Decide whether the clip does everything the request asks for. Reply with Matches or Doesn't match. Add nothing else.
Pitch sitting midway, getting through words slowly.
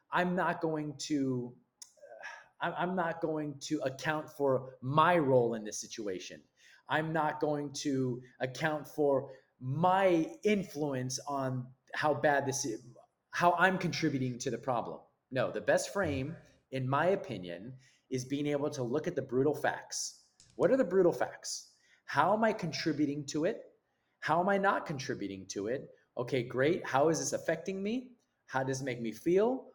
Doesn't match